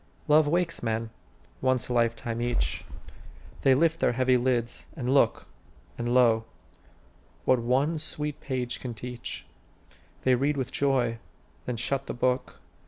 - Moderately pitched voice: No, low, 125 Hz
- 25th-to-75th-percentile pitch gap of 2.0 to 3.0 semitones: Yes, narrow, 2.6 semitones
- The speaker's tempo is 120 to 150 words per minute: Yes, average, 140 wpm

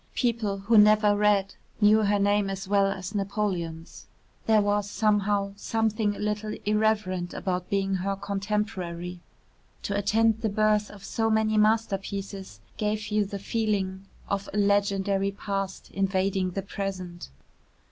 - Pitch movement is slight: Yes, narrow, 1.5 semitones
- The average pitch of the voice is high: Yes, high, 200 Hz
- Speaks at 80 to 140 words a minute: Yes, slow, 135 wpm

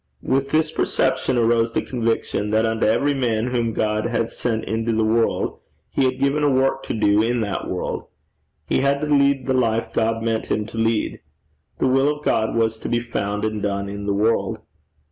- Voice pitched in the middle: No, low, 115 Hz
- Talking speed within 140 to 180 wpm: No, average, 200 wpm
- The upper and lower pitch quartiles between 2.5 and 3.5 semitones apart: Yes, average, 3.0 semitones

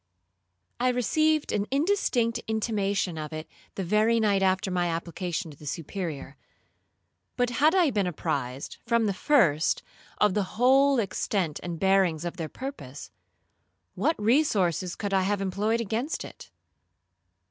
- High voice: Yes, high, 200 Hz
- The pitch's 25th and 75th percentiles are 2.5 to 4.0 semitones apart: No, wide, 5.4 semitones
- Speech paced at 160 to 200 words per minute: No, average, 140 wpm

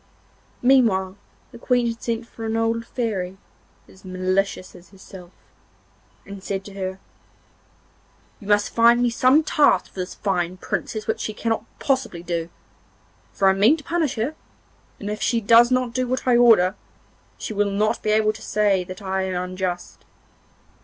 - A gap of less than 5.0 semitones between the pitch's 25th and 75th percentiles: Yes, average, 3.8 semitones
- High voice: Yes, high, 210 Hz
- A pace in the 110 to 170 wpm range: Yes, average, 165 wpm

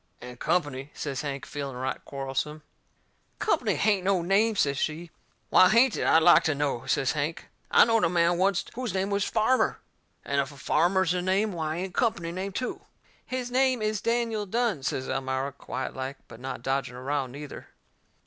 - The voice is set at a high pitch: No, medium, 170 Hz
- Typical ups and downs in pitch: No, wide, 6.7 semitones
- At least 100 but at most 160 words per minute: No, average, 190 wpm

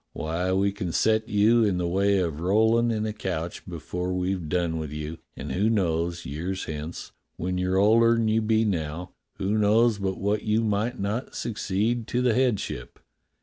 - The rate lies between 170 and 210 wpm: Yes, average, 185 wpm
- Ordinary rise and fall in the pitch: Yes, average, 3.9 semitones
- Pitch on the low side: Yes, low, 100 Hz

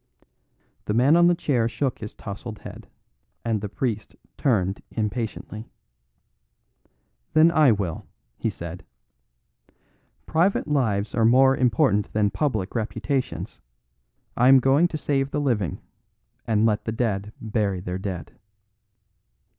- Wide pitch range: No, average, 4.6 semitones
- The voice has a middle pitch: No, low, 115 Hz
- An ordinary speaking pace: No, slow, 125 wpm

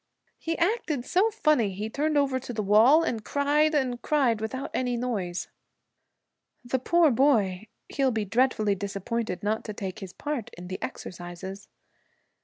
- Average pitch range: No, wide, 5.9 semitones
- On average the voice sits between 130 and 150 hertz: No, high, 240 Hz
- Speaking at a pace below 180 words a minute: Yes, average, 155 wpm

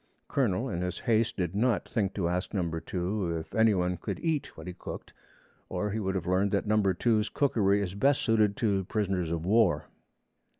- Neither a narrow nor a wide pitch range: Yes, average, 3.4 semitones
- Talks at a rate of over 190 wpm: Yes, average, 200 wpm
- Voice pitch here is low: Yes, low, 100 Hz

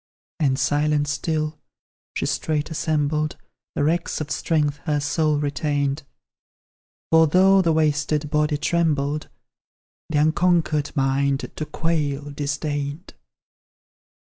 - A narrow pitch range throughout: Yes, narrow, 1.5 semitones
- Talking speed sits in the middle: No, slow, 105 wpm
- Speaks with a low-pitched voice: No, medium, 150 Hz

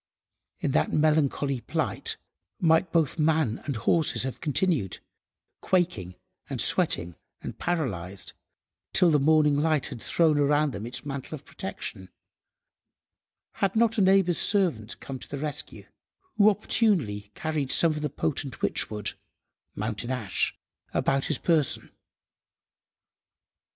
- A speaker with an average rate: No, slow, 115 wpm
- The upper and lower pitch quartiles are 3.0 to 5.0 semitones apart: No, wide, 5.4 semitones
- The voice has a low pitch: No, medium, 145 Hz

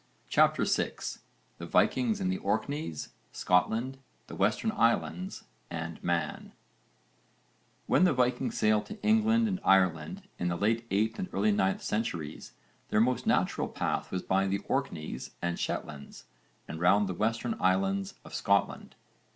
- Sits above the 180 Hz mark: No, low, 105 Hz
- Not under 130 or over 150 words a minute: Yes, average, 145 wpm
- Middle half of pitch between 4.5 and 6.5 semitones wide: Yes, wide, 5.5 semitones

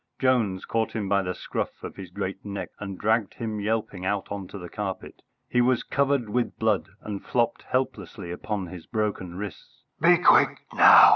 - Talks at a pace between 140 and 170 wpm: No, average, 185 wpm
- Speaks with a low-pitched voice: Yes, low, 105 Hz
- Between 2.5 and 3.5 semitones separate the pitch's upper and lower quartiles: Yes, average, 2.9 semitones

